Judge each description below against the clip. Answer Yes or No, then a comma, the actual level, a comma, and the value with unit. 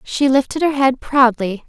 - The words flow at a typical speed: Yes, average, 180 wpm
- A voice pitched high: Yes, very high, 260 Hz